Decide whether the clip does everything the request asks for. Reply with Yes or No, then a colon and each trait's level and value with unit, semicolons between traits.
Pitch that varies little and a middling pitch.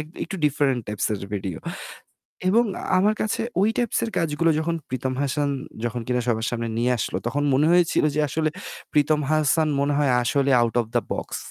No: average, 4.5 semitones; medium, 145 Hz